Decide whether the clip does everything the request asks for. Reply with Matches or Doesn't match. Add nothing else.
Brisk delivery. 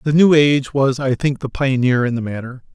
Matches